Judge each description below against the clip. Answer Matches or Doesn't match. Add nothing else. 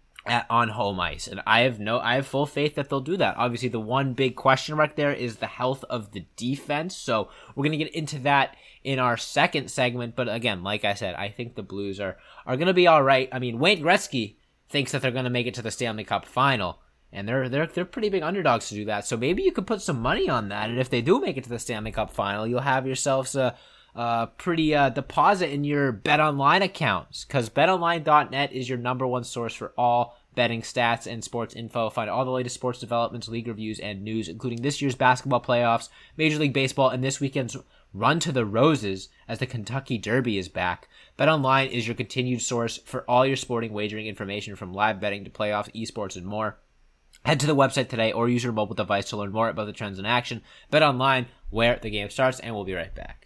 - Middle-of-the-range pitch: Doesn't match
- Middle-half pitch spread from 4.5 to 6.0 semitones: Doesn't match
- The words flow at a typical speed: Doesn't match